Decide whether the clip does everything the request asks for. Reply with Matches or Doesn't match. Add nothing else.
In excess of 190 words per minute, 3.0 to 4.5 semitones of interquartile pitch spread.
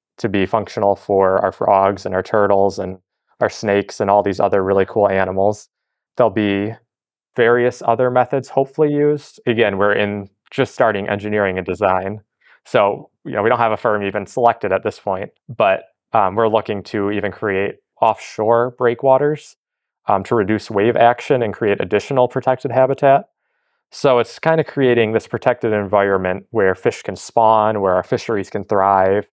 Doesn't match